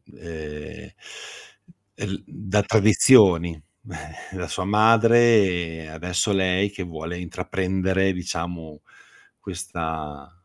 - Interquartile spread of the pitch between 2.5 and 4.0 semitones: Yes, average, 2.9 semitones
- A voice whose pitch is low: Yes, very low, 90 Hz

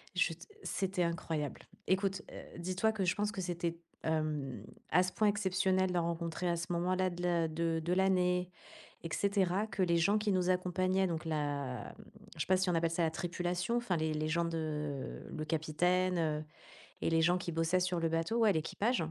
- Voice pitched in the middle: Yes, medium, 175 Hz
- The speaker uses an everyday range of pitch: No, narrow, 2.3 semitones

